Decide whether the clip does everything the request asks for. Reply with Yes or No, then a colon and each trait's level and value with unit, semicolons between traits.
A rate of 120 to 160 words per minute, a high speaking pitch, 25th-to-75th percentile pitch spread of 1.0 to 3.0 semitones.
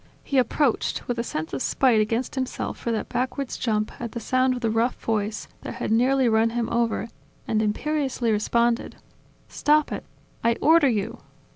No: average, 175 wpm; high, 235 Hz; average, 2.7 semitones